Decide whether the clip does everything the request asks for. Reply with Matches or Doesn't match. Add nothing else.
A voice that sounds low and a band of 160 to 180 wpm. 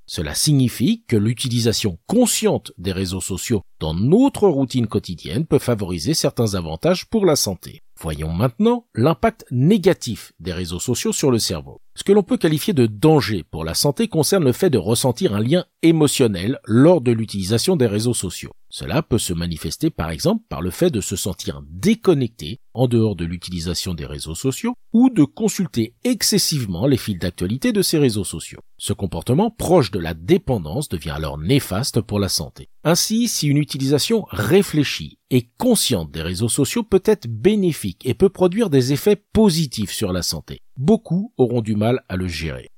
Matches